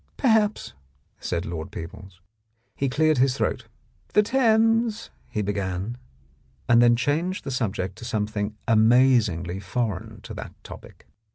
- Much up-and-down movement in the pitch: Yes, wide, 8.0 semitones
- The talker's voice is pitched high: No, low, 120 Hz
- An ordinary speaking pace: No, slow, 130 wpm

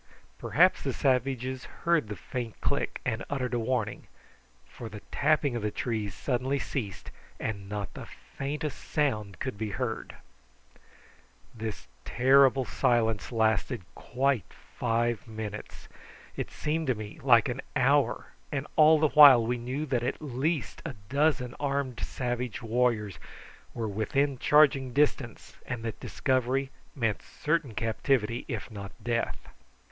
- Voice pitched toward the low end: Yes, low, 125 Hz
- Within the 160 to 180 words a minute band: No, slow, 135 wpm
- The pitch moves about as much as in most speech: Yes, average, 3.7 semitones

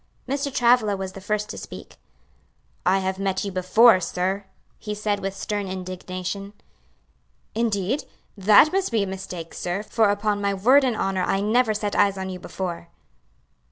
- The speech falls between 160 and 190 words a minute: Yes, average, 165 wpm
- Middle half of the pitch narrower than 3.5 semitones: Yes, narrow, 2.4 semitones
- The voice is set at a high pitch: Yes, high, 200 Hz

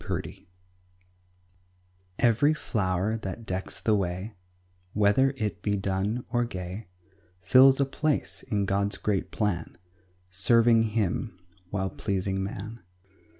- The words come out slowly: Yes, slow, 115 wpm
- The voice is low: Yes, low, 105 Hz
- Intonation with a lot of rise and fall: No, average, 3.4 semitones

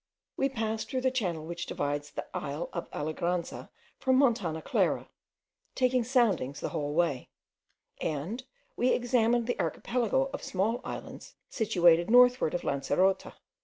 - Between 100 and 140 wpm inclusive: Yes, slow, 135 wpm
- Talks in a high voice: Yes, high, 200 Hz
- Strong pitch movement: Yes, wide, 7.2 semitones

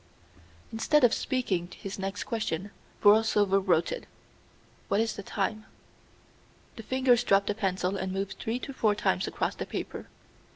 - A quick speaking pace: No, average, 155 wpm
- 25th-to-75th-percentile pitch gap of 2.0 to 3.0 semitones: Yes, narrow, 2.6 semitones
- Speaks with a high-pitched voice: Yes, high, 205 Hz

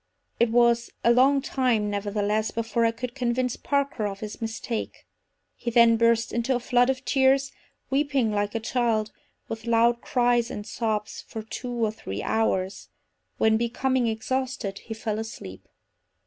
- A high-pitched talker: Yes, high, 230 Hz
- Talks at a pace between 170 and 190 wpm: No, average, 155 wpm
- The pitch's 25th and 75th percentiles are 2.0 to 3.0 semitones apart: Yes, narrow, 2.4 semitones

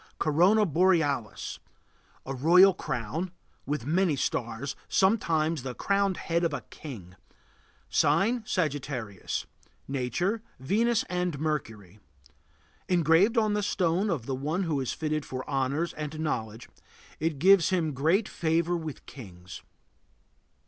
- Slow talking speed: Yes, slow, 120 wpm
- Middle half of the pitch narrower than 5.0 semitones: No, average, 5.3 semitones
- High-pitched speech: No, medium, 155 Hz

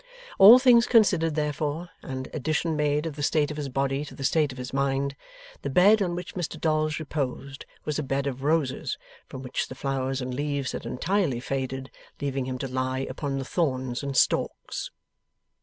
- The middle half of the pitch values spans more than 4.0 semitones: No, average, 3.0 semitones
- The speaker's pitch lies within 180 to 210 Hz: No, medium, 140 Hz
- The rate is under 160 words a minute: No, average, 190 wpm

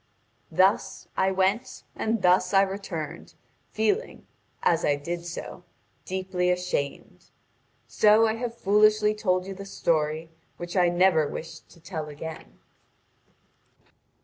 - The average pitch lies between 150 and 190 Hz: Yes, medium, 185 Hz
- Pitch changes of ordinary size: Yes, average, 3.5 semitones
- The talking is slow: Yes, slow, 120 wpm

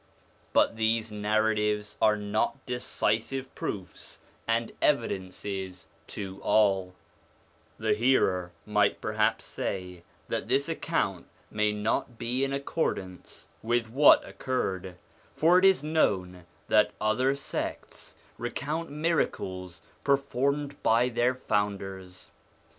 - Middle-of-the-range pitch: No, low, 110 Hz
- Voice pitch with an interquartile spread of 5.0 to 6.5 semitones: Yes, average, 5.3 semitones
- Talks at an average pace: No, slow, 110 wpm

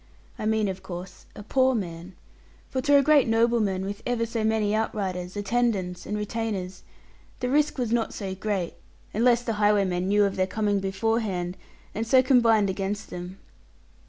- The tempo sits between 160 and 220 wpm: Yes, average, 165 wpm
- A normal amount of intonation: Yes, average, 3.3 semitones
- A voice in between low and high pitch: No, high, 210 Hz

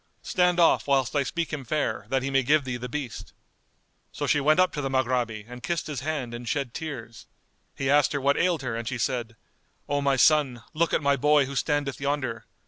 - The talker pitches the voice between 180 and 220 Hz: No, medium, 140 Hz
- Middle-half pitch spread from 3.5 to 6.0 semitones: No, average, 3.1 semitones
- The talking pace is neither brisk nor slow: No, fast, 225 wpm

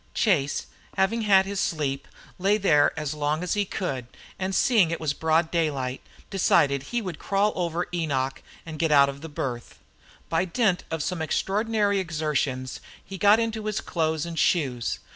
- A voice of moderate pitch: Yes, medium, 165 Hz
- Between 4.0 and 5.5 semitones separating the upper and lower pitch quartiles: Yes, average, 5.0 semitones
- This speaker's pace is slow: No, average, 170 wpm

